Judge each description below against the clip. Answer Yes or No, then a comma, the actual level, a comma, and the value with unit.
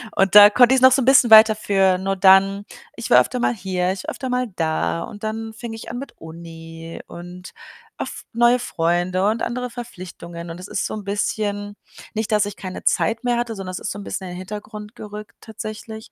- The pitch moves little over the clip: No, average, 3.4 semitones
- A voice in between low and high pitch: No, high, 205 Hz